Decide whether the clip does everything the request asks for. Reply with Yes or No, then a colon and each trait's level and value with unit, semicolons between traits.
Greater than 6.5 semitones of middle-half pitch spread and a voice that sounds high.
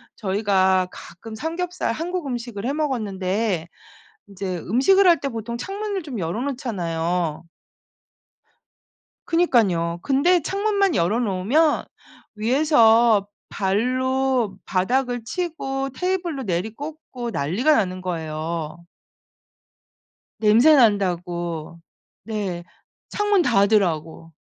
Yes: wide, 7.3 semitones; high, 225 Hz